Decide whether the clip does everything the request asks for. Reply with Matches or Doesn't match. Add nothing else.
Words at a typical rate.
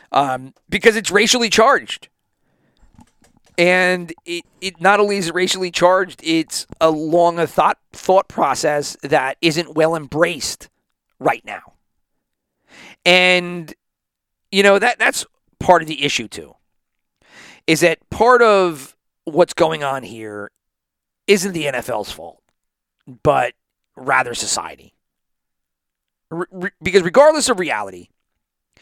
Doesn't match